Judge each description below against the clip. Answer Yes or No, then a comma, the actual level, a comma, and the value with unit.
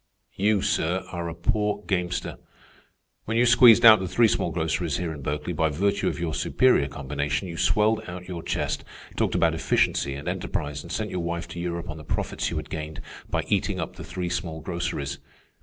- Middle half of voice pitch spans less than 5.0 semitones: Yes, average, 3.4 semitones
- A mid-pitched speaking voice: No, very low, 85 Hz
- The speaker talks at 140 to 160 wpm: No, average, 200 wpm